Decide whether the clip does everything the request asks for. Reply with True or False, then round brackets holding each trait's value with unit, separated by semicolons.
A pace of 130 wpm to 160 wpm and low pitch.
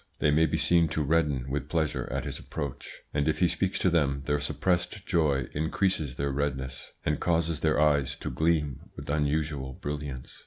False (185 wpm; 75 Hz)